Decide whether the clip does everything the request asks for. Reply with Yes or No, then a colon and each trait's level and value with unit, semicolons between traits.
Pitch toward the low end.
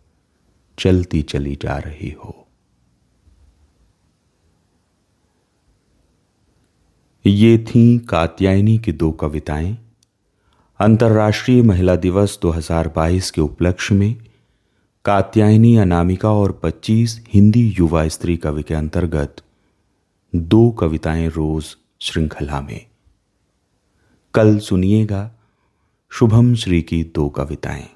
Yes: very low, 90 Hz